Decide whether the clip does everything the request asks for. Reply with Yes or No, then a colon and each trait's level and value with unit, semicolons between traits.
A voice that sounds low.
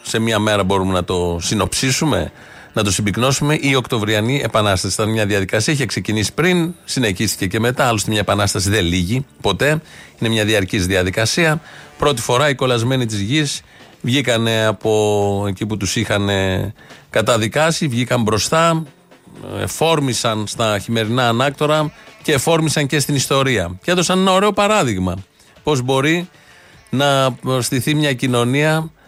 Yes: low, 120 Hz